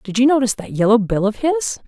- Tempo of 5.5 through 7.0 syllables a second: Yes, 6.2 syllables/s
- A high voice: Yes, high, 225 Hz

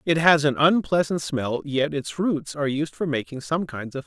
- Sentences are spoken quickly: Yes, fast, 235 wpm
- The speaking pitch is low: No, medium, 145 Hz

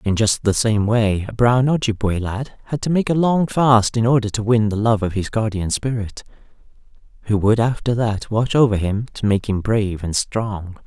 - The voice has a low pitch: Yes, low, 110 Hz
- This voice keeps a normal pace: No, fast, 210 wpm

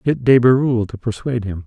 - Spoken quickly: Yes, fast, 215 wpm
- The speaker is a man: Yes, male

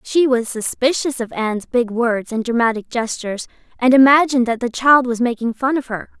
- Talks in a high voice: Yes, high, 245 Hz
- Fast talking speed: No, average, 195 wpm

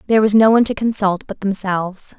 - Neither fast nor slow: No, fast, 220 wpm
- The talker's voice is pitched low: No, high, 205 Hz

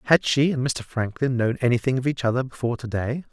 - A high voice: No, low, 125 Hz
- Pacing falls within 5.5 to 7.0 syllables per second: Yes, 6.2 syllables/s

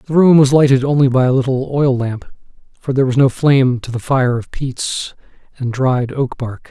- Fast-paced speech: Yes, fast, 215 wpm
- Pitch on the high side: No, low, 130 Hz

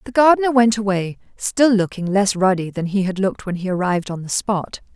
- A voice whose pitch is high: Yes, high, 200 Hz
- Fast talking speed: Yes, fast, 220 wpm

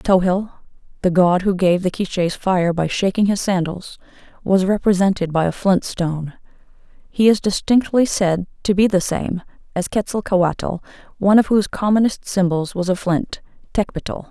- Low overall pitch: No, high, 190 Hz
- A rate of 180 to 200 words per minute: No, average, 155 wpm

